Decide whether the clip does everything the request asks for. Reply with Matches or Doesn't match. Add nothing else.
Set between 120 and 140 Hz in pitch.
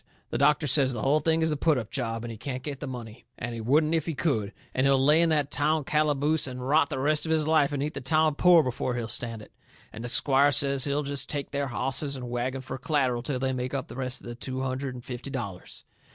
Matches